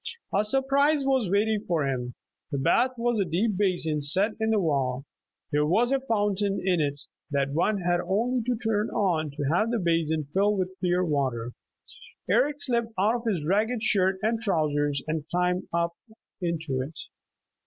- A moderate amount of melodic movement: No, wide, 6.2 semitones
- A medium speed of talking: Yes, average, 175 wpm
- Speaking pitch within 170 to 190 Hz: Yes, medium, 185 Hz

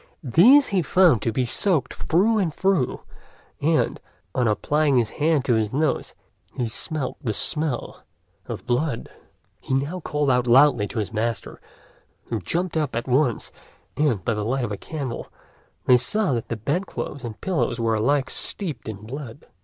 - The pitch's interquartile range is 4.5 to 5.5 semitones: Yes, average, 5.1 semitones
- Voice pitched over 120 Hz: Yes, low, 135 Hz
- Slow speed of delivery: No, average, 170 wpm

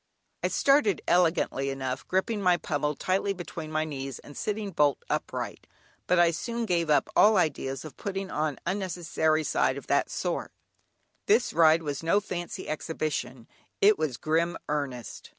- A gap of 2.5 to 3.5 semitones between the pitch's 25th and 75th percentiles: No, average, 4.2 semitones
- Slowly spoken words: No, average, 155 wpm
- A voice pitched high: No, medium, 160 Hz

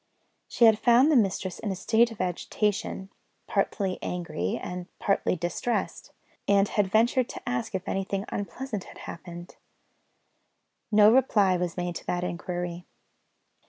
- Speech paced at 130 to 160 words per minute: Yes, average, 140 wpm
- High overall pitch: Yes, high, 195 Hz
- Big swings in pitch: No, average, 3.6 semitones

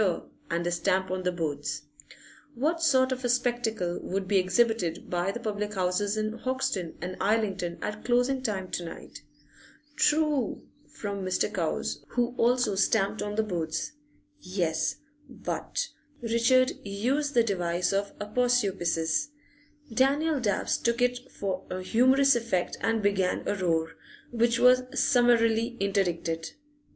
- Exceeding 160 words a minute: No, slow, 135 wpm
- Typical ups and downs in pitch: Yes, average, 5.0 semitones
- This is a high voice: Yes, high, 210 Hz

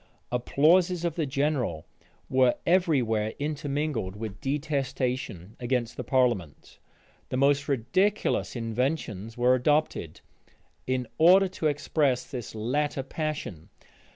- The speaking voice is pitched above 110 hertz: Yes, low, 135 Hz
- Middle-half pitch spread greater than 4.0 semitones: Yes, average, 4.4 semitones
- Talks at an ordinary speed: No, slow, 110 wpm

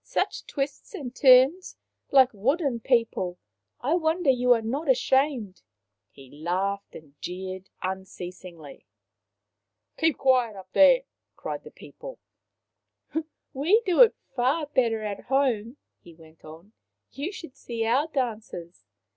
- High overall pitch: Yes, high, 245 Hz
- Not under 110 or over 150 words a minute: Yes, average, 140 wpm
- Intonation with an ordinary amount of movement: No, wide, 7.1 semitones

